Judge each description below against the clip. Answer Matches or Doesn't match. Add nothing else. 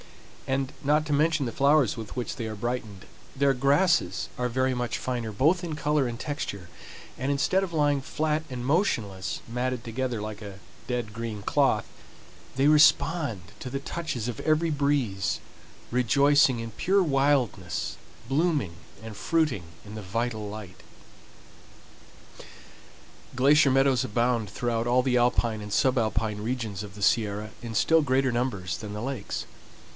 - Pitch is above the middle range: Doesn't match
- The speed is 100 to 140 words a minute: Doesn't match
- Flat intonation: Doesn't match